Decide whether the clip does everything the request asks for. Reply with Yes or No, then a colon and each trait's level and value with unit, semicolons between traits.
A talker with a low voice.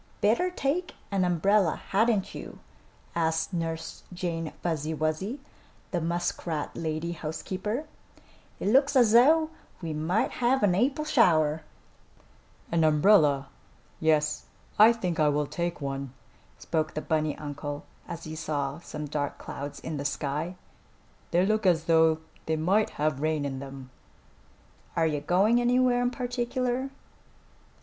No: medium, 165 Hz